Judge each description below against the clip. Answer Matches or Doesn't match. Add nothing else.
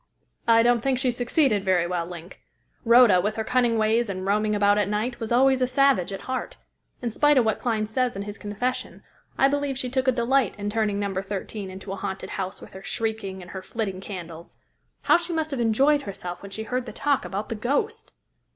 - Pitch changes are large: Doesn't match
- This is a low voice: Doesn't match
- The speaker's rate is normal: Doesn't match